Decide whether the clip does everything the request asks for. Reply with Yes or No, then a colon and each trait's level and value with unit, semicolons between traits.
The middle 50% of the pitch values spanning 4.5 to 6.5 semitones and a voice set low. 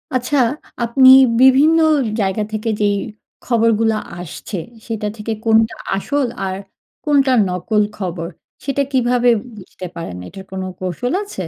No: average, 5.1 semitones; high, 225 Hz